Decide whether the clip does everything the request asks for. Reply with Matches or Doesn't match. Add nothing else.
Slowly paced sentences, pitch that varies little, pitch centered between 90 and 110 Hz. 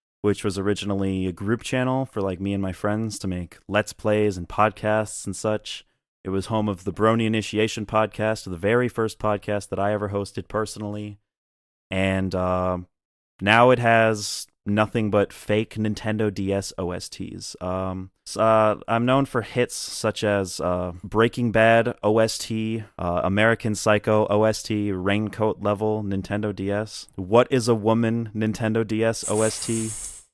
Doesn't match